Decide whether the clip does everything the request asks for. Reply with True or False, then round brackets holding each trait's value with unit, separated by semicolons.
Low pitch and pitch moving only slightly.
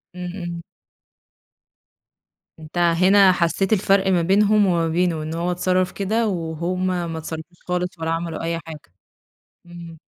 False (175 Hz; 2.0 semitones)